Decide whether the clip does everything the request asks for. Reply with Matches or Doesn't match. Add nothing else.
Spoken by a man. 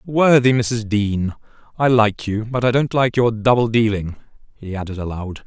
Matches